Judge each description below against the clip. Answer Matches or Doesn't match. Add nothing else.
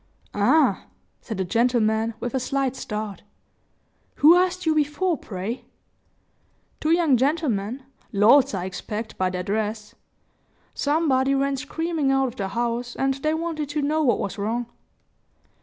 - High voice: Matches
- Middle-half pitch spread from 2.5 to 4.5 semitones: Doesn't match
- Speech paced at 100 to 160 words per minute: Matches